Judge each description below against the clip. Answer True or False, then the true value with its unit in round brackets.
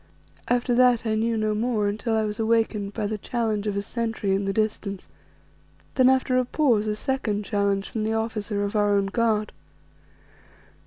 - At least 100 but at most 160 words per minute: False (180 wpm)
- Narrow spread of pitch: True (2.1 semitones)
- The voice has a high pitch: True (215 Hz)